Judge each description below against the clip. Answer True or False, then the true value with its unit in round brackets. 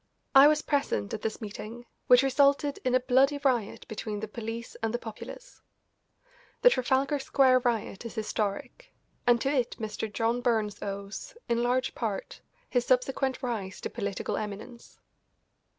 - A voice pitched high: True (240 Hz)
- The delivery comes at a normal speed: True (150 wpm)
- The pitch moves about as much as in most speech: True (3.6 semitones)